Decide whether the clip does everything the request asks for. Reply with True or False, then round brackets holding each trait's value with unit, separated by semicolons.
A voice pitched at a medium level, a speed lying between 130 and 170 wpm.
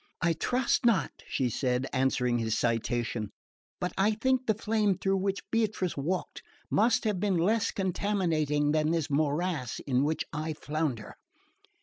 True (165 Hz; 145 wpm)